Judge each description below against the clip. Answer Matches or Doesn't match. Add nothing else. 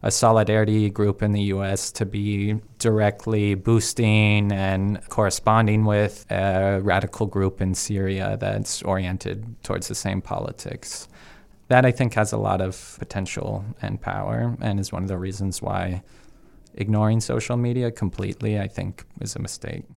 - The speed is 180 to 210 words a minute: Doesn't match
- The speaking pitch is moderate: Doesn't match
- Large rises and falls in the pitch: Doesn't match